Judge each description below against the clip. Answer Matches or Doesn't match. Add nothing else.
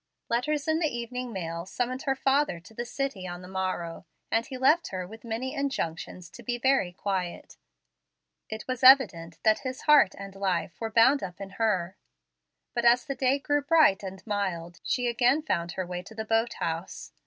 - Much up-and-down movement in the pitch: Matches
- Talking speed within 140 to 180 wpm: Doesn't match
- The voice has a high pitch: Matches